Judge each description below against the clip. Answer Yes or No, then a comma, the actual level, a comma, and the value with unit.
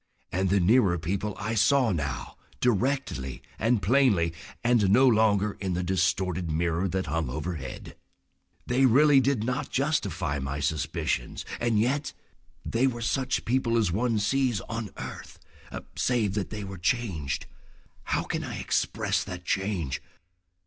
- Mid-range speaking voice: No, low, 100 Hz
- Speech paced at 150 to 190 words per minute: No, average, 140 wpm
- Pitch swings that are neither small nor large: No, wide, 5.9 semitones